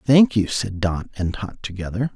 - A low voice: Yes, low, 105 Hz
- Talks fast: No, average, 195 wpm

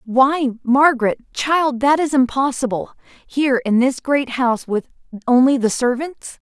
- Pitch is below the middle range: No, very high, 260 Hz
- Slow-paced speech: Yes, slow, 130 wpm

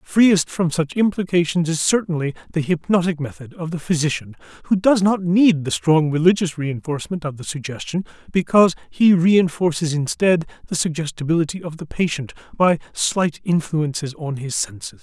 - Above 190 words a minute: No, average, 150 wpm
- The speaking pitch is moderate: Yes, medium, 165 Hz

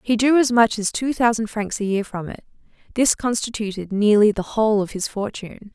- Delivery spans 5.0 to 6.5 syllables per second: Yes, 5.5 syllables/s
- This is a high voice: Yes, high, 220 Hz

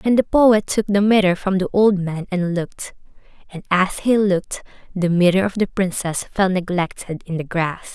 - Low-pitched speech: No, high, 190 Hz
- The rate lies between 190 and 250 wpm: Yes, average, 195 wpm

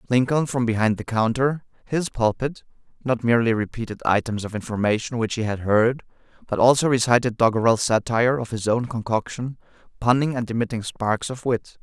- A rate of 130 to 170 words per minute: Yes, average, 150 wpm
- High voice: No, low, 120 Hz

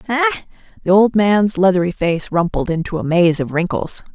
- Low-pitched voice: No, high, 190 Hz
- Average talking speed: Yes, average, 175 wpm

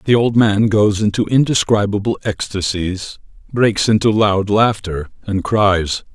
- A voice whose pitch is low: Yes, low, 105 Hz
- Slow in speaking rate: Yes, slow, 125 wpm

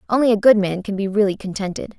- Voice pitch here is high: Yes, high, 205 Hz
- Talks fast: Yes, fast, 240 wpm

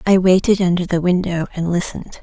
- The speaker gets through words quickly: No, average, 190 wpm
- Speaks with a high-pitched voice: No, medium, 180 Hz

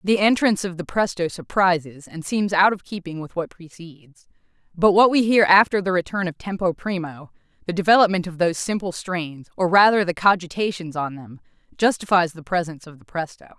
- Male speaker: No, female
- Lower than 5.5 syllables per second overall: No, 5.6 syllables/s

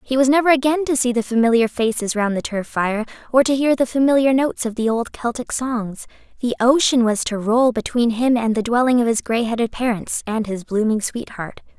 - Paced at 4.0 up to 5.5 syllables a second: Yes, 5.4 syllables/s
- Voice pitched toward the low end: No, high, 240 Hz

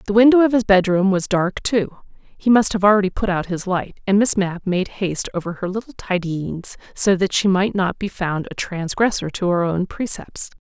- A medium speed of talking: No, fast, 215 wpm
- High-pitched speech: Yes, high, 195 Hz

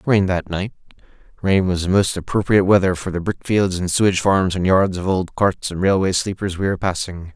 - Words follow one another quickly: Yes, fast, 220 wpm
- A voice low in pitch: Yes, very low, 95 Hz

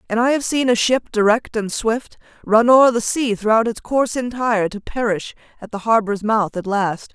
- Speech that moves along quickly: Yes, fast, 210 wpm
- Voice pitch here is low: No, high, 225 Hz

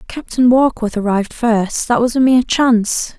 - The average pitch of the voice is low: No, high, 235 Hz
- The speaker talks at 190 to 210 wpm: No, average, 170 wpm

